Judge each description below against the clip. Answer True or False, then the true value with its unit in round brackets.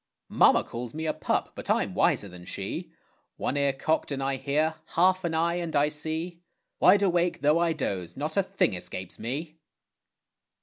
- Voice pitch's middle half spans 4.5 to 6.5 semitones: False (4.0 semitones)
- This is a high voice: False (155 Hz)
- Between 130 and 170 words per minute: False (180 wpm)